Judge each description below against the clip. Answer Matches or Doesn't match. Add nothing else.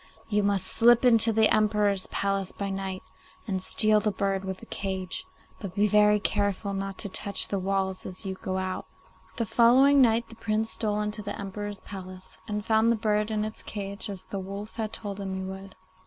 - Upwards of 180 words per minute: Matches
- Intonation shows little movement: Matches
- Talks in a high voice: Matches